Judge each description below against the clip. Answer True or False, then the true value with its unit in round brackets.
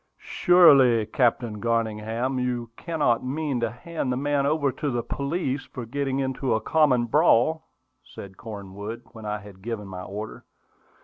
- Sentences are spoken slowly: False (150 wpm)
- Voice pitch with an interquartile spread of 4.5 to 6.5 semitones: False (4.1 semitones)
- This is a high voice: False (120 Hz)